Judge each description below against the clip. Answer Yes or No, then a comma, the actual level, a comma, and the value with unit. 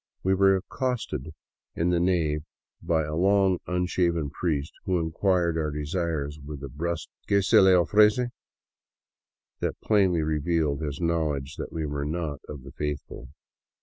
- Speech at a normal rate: Yes, average, 160 wpm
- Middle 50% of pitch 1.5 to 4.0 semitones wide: Yes, average, 3.7 semitones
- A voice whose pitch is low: Yes, very low, 85 Hz